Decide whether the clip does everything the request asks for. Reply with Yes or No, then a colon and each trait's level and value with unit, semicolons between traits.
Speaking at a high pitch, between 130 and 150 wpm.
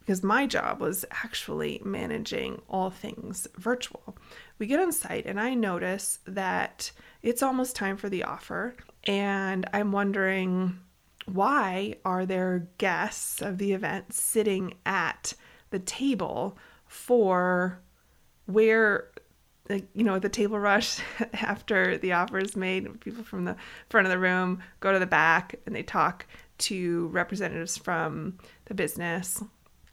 Yes: high, 195 Hz; slow, 135 wpm